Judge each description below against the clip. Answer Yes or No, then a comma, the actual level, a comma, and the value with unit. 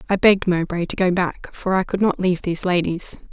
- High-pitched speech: No, medium, 180 Hz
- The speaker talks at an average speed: No, fast, 235 wpm